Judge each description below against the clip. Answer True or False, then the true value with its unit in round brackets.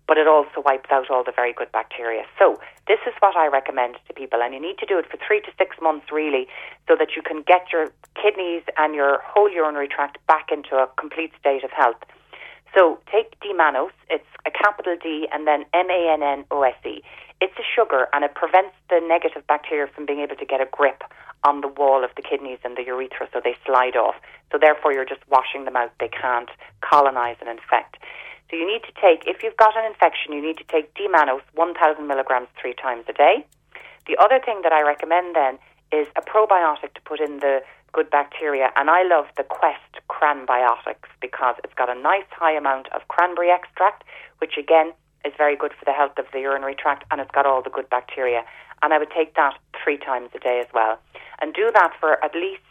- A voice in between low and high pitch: True (150 Hz)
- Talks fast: True (215 wpm)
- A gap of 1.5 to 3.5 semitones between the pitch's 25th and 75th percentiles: False (4.1 semitones)